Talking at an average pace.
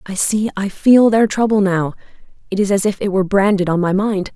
No: fast, 220 wpm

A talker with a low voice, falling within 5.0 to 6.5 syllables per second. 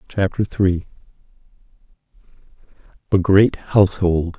No: very low, 95 Hz; 4.0 syllables/s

